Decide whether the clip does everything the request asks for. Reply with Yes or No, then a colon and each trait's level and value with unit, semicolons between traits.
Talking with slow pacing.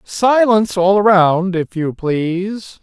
Yes: slow, 125 wpm